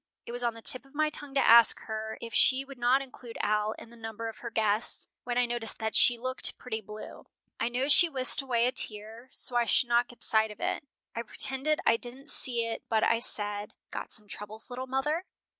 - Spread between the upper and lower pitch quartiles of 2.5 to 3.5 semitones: Yes, average, 2.8 semitones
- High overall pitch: Yes, high, 235 Hz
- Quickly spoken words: Yes, fast, 230 wpm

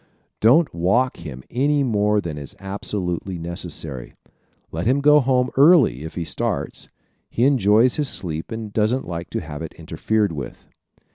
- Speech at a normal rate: Yes, average, 155 wpm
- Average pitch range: No, wide, 7.4 semitones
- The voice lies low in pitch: Yes, low, 105 Hz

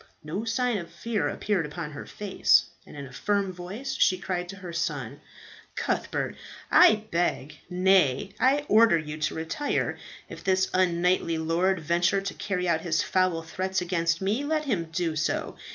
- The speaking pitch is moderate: Yes, medium, 180 Hz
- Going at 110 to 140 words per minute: No, average, 170 wpm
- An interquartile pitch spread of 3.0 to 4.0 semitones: Yes, average, 3.4 semitones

